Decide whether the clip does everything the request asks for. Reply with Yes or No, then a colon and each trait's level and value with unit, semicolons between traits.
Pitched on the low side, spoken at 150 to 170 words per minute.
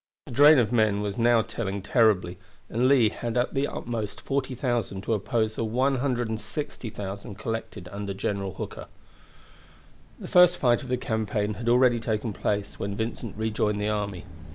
Yes: low, 110 Hz; average, 155 wpm